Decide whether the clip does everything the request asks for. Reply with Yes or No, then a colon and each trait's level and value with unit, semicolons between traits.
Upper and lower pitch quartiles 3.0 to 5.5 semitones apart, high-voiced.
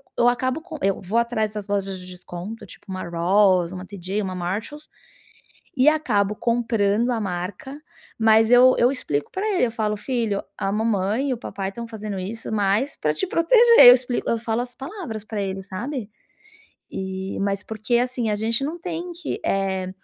Yes: average, 4.2 semitones; high, 220 Hz